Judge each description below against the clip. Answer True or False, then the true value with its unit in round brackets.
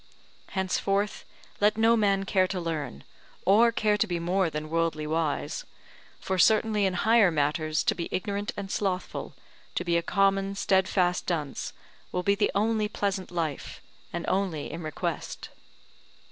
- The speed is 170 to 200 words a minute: False (150 wpm)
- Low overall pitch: False (190 Hz)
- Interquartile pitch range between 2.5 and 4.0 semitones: True (3.4 semitones)